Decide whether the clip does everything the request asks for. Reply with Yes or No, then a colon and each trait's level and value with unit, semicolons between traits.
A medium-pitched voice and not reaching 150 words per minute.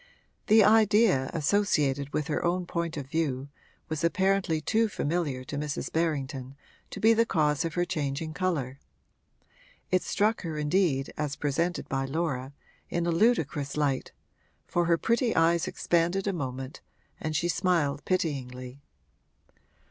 Yes: medium, 160 Hz; average, 140 wpm